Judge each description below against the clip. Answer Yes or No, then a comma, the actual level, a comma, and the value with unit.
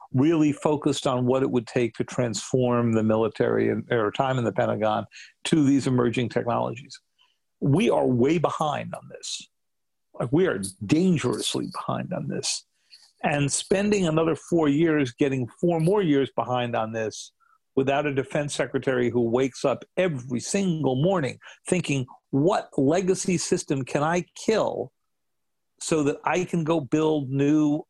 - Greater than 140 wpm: Yes, average, 150 wpm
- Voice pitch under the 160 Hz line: Yes, medium, 140 Hz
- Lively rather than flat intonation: No, average, 4.9 semitones